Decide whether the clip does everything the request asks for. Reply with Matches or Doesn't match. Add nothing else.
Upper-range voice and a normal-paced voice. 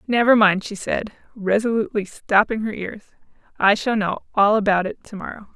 Matches